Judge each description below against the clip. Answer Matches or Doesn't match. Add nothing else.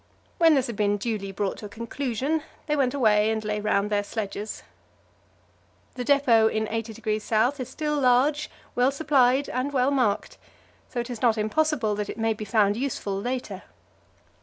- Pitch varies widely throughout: Doesn't match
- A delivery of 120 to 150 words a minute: Doesn't match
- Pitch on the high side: Matches